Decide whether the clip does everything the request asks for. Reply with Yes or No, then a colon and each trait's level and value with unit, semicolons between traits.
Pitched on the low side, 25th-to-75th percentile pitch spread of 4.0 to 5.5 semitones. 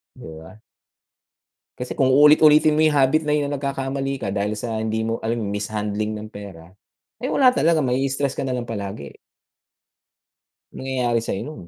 Yes: low, 125 Hz; average, 4.9 semitones